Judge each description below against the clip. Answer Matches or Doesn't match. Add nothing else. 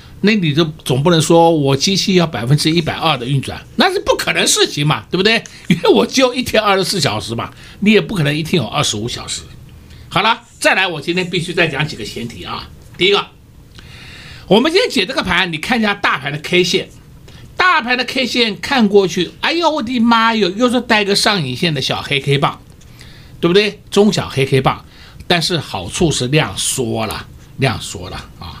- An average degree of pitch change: Doesn't match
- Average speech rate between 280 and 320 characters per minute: Matches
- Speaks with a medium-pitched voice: Matches